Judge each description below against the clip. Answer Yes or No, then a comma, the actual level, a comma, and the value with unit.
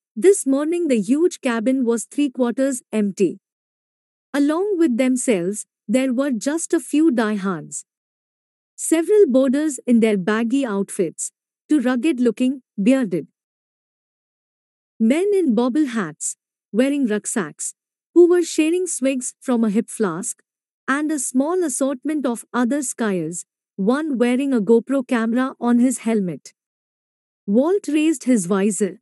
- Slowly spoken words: Yes, slow, 125 wpm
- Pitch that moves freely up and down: No, average, 4.4 semitones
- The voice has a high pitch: Yes, very high, 255 Hz